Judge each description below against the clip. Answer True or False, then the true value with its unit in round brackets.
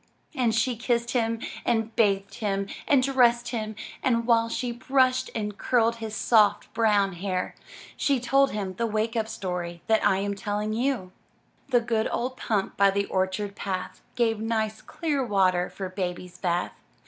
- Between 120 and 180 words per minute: True (170 wpm)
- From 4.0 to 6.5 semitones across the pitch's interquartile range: False (3.2 semitones)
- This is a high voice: True (220 Hz)